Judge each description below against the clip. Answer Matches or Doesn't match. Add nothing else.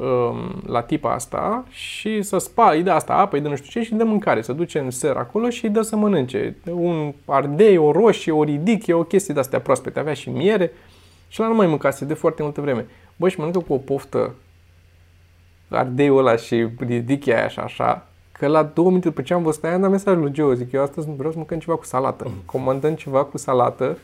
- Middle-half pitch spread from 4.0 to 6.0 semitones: Matches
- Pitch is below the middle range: Doesn't match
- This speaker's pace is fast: Matches